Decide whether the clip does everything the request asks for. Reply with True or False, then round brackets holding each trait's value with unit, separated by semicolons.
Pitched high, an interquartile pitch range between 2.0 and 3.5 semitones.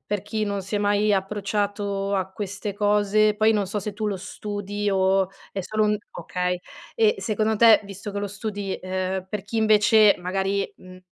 False (205 Hz; 1.5 semitones)